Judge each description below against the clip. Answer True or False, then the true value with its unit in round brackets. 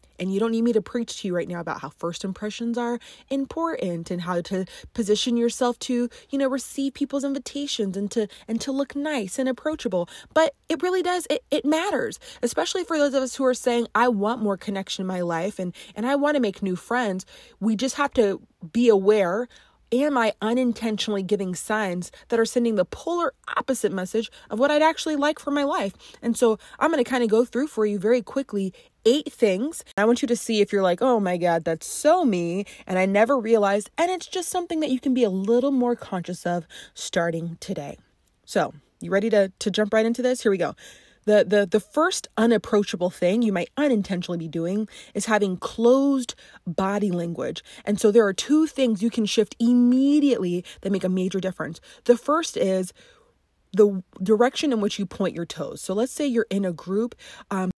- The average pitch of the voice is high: True (225 Hz)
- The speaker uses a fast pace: True (210 wpm)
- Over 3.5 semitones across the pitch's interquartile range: True (5.4 semitones)